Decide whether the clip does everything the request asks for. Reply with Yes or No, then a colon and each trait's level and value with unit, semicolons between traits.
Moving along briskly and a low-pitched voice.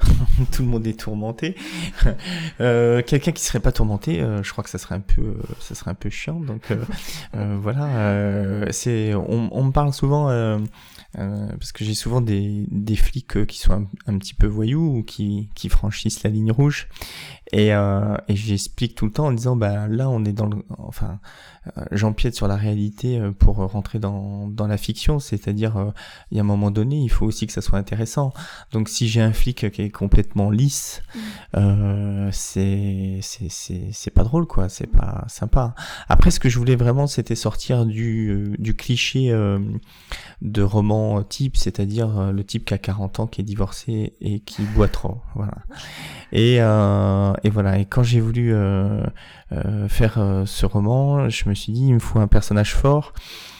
No: average, 200 wpm; low, 105 Hz